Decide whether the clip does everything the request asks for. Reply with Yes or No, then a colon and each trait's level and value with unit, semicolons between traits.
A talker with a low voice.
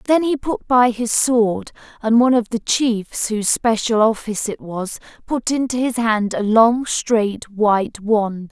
No: high, 225 Hz